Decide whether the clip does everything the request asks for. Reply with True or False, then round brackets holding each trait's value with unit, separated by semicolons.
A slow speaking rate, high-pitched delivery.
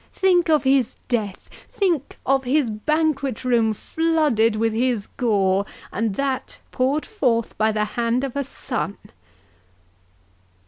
True (125 wpm; 250 Hz)